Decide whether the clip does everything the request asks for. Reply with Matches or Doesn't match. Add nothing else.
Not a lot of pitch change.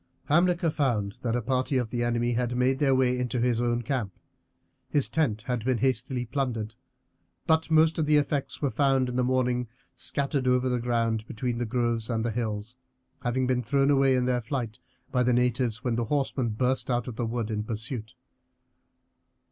Matches